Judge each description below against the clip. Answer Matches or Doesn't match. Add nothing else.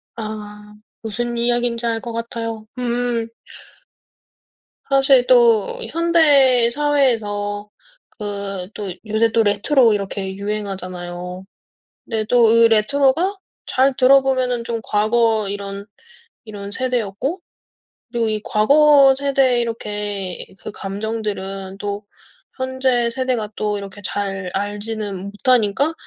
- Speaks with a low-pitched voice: Doesn't match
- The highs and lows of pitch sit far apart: Doesn't match